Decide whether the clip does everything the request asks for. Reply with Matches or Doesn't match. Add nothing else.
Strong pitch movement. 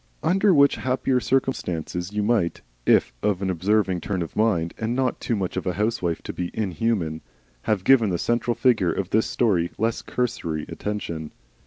Doesn't match